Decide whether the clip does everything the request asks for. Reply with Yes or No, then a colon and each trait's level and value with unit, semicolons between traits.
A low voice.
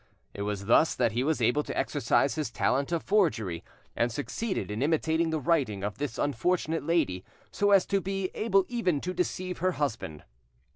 No: medium, 155 Hz